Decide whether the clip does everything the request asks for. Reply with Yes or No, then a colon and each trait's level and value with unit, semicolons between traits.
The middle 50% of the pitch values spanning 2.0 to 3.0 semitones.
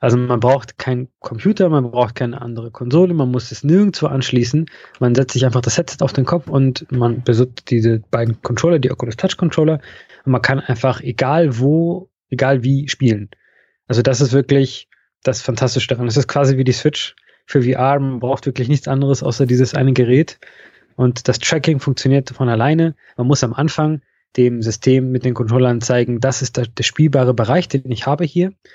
Yes: narrow, 2.6 semitones